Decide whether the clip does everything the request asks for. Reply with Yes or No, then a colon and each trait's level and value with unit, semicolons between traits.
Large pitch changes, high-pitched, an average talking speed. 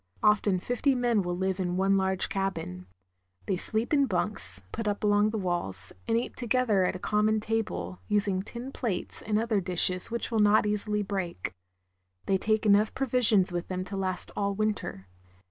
No: average, 2.9 semitones; high, 205 Hz; average, 180 wpm